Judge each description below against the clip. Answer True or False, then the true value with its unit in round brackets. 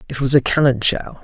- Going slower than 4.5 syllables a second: False (5.7 syllables/s)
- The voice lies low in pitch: True (130 Hz)